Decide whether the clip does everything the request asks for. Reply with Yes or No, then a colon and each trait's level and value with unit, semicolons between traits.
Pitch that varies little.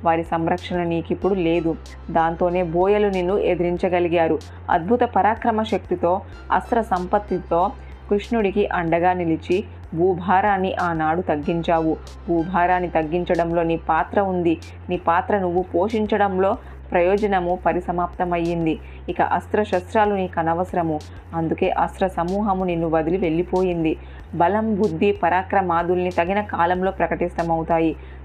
Yes: narrow, 2.2 semitones